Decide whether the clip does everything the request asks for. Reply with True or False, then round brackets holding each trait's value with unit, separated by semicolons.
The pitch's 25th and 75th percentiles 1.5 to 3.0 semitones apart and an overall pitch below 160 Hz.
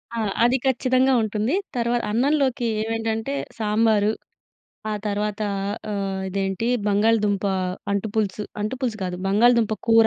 False (2.5 semitones; 220 Hz)